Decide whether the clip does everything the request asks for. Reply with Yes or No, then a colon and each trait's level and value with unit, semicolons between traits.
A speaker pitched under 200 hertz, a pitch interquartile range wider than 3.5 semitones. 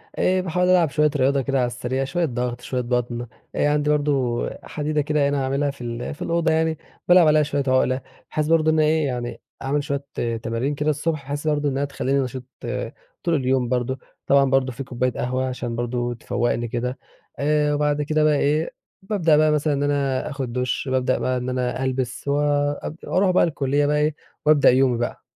No: medium, 140 Hz; average, 3.0 semitones